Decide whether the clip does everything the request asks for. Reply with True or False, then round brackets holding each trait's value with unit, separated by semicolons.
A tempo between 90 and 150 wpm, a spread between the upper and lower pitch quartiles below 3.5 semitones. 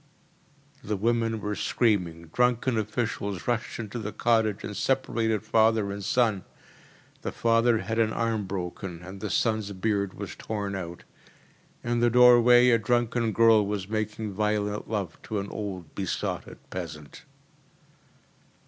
True (140 wpm; 2.6 semitones)